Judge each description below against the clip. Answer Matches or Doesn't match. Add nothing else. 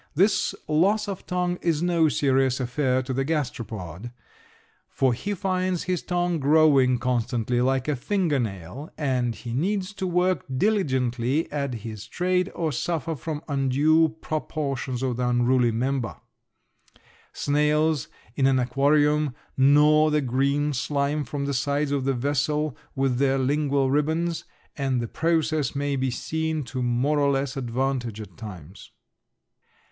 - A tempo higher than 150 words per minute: Doesn't match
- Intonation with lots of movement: Doesn't match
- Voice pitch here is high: Doesn't match